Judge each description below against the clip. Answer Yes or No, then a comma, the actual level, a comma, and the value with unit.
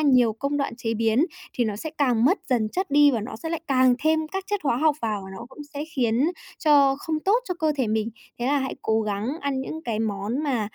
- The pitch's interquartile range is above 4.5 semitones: Yes, average, 5.1 semitones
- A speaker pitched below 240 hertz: No, very high, 265 Hz